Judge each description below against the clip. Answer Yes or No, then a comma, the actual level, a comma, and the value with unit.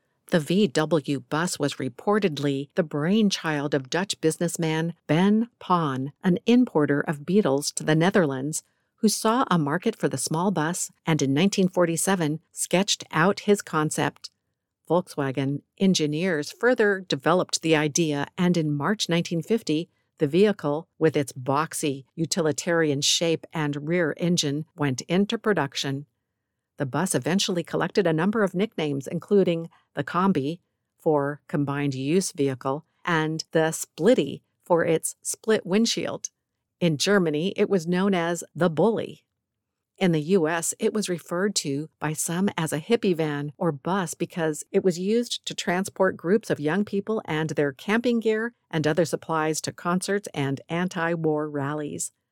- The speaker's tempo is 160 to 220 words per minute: No, average, 145 wpm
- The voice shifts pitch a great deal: No, average, 4.3 semitones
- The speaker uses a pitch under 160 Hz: No, medium, 165 Hz